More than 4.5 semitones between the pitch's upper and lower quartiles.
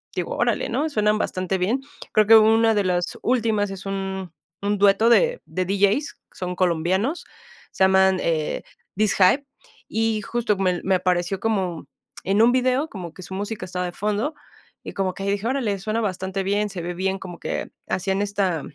No: average, 3.0 semitones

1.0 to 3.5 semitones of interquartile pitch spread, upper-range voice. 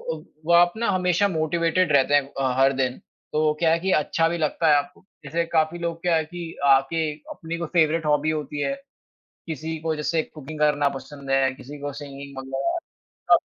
No: average, 2.8 semitones; medium, 155 Hz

